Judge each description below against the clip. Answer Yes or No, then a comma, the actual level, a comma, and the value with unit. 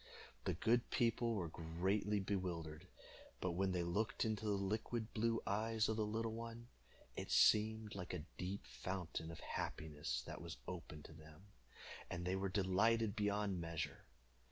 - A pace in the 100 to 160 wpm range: Yes, average, 155 wpm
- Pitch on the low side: Yes, low, 100 Hz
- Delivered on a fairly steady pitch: No, average, 4.0 semitones